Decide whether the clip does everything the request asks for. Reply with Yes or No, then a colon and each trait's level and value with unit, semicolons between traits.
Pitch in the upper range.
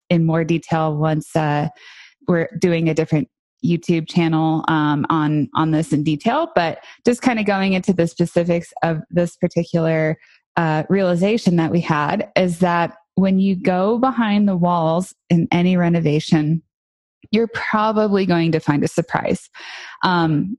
No: medium, 170 Hz